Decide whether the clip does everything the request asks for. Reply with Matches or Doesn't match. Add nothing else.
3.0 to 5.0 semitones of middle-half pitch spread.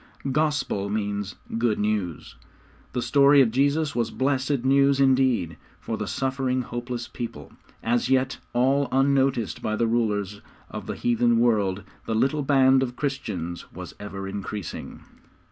Matches